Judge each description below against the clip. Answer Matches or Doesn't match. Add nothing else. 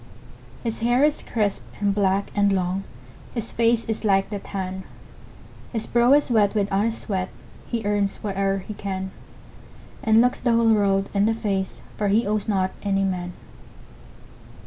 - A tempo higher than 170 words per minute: Doesn't match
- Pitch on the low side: Doesn't match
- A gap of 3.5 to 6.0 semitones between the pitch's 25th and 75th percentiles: Doesn't match